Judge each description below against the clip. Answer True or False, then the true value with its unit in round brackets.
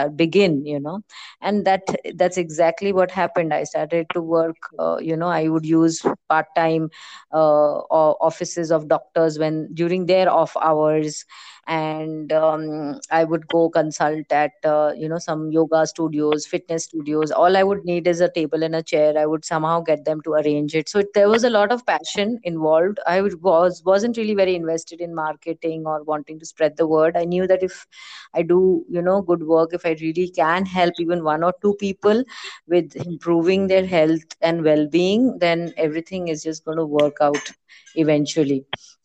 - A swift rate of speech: False (185 wpm)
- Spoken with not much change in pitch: True (2.3 semitones)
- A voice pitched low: False (165 Hz)